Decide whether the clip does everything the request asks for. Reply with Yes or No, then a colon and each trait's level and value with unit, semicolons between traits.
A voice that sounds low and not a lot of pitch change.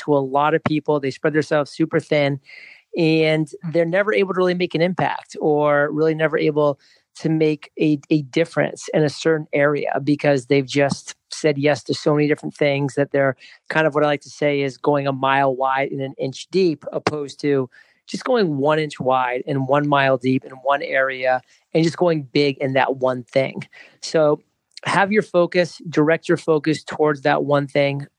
No: medium, 150 Hz; narrow, 2.3 semitones